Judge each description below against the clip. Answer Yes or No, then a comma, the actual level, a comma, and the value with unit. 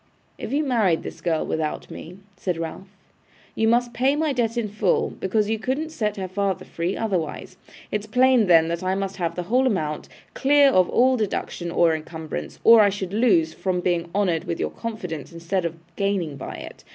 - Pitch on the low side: No, high, 195 Hz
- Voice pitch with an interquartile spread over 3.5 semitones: Yes, average, 5.1 semitones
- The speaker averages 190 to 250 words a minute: Yes, average, 195 wpm